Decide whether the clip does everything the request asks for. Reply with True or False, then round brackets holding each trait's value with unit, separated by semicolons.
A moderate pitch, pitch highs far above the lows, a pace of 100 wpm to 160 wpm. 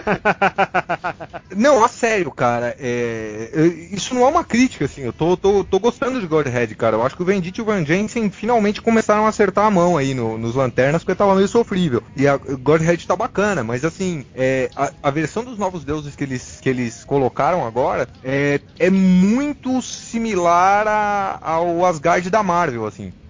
False (175 Hz; 7.1 semitones; 185 wpm)